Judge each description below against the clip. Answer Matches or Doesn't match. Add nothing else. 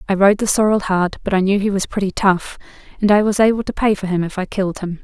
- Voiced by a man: Doesn't match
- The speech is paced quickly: Matches